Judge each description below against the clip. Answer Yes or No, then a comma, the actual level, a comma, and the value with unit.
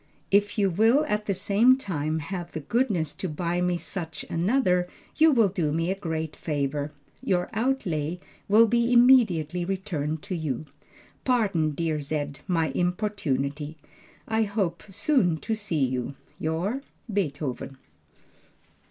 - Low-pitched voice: No, medium, 180 Hz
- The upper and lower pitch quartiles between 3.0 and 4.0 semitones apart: No, average, 5.1 semitones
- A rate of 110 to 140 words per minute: Yes, slow, 135 wpm